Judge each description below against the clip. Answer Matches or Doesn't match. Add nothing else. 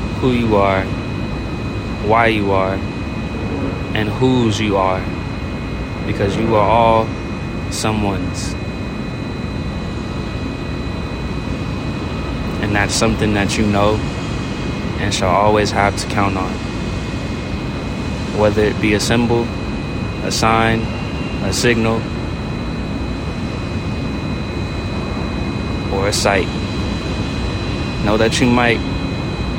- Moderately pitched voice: Doesn't match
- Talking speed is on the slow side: Matches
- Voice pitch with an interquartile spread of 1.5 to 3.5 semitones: Matches